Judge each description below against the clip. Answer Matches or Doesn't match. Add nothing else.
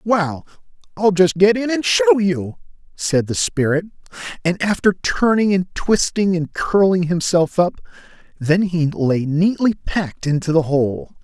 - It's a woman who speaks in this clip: Doesn't match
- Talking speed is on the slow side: Doesn't match